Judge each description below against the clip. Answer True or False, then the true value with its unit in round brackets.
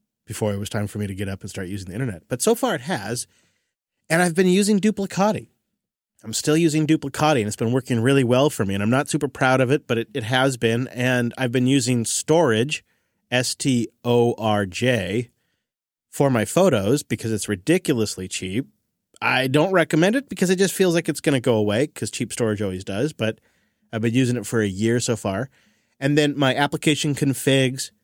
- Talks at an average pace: False (210 wpm)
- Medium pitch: False (130 Hz)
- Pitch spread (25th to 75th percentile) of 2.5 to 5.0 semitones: False (5.5 semitones)